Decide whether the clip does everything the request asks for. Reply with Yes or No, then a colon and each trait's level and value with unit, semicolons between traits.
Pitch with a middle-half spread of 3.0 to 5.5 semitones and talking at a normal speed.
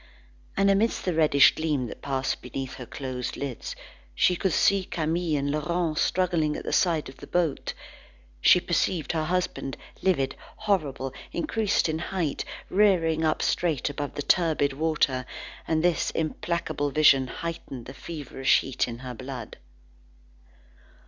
Yes: average, 4.3 semitones; average, 150 wpm